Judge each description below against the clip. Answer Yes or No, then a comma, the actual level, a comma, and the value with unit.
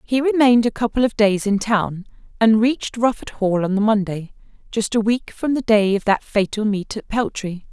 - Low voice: No, high, 220 Hz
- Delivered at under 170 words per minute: No, average, 200 wpm